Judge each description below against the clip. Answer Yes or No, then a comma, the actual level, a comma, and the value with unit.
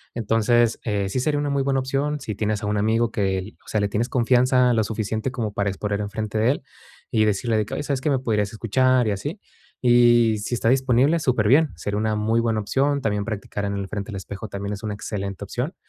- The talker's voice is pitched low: Yes, low, 110 Hz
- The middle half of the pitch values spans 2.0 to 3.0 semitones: No, average, 3.6 semitones